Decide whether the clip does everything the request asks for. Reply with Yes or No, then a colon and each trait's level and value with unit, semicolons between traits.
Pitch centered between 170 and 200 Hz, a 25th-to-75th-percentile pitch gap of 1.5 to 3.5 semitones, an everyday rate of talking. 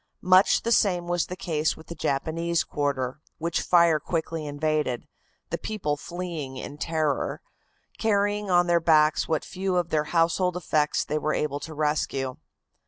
No: medium, 160 Hz; average, 2.9 semitones; average, 160 wpm